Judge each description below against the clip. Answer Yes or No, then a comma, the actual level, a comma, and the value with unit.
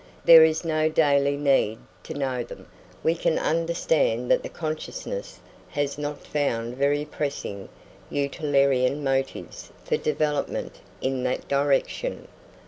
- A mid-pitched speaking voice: Yes, medium, 145 Hz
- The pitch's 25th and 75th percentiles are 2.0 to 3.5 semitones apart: Yes, narrow, 2.6 semitones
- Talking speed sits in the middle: No, slow, 130 wpm